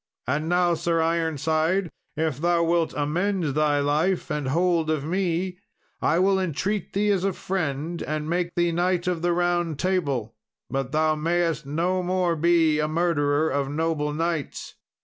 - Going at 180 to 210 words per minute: No, average, 160 wpm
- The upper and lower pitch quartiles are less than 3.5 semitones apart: Yes, narrow, 2.6 semitones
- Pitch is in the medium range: Yes, medium, 165 Hz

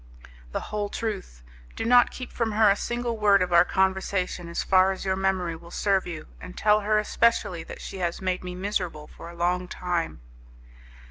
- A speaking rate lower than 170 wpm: No, average, 195 wpm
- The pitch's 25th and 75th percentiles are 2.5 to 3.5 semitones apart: Yes, average, 2.9 semitones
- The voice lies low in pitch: No, high, 190 Hz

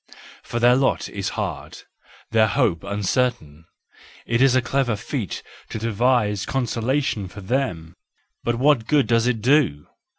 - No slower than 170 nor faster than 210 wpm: No, average, 145 wpm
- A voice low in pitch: Yes, low, 120 Hz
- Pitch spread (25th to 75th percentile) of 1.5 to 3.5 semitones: No, average, 3.9 semitones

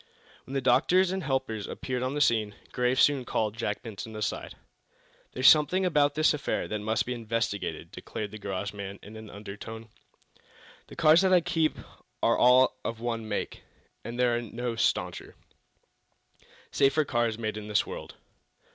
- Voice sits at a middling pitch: No, low, 120 Hz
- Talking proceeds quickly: No, average, 165 wpm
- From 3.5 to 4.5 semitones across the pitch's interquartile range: Yes, average, 4.2 semitones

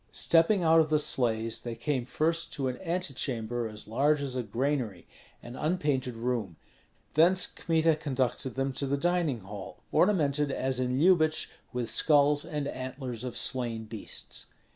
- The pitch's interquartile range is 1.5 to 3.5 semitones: No, average, 4.3 semitones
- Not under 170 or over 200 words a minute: No, average, 155 wpm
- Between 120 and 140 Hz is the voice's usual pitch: Yes, low, 135 Hz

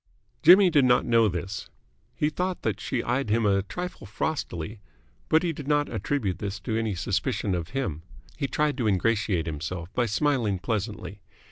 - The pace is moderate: Yes, average, 170 wpm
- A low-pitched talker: Yes, low, 110 Hz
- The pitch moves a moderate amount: No, wide, 6.8 semitones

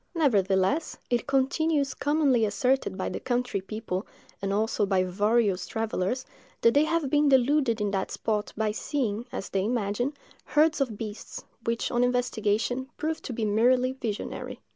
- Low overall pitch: No, high, 235 Hz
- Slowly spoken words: No, average, 155 wpm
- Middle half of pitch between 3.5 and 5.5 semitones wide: Yes, average, 4.4 semitones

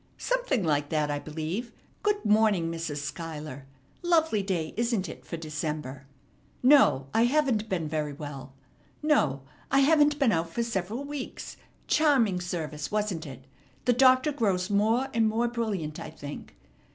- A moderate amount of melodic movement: No, wide, 8.0 semitones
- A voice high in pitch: Yes, high, 195 Hz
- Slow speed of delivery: No, average, 150 wpm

